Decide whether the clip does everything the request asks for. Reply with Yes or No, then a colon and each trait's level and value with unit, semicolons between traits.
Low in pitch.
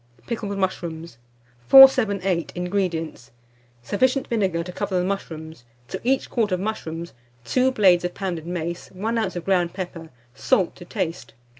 No: medium, 180 Hz